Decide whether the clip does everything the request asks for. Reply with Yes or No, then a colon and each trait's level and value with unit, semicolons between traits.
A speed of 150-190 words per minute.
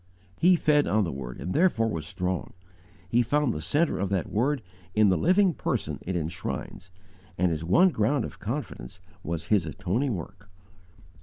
Yes: average, 170 wpm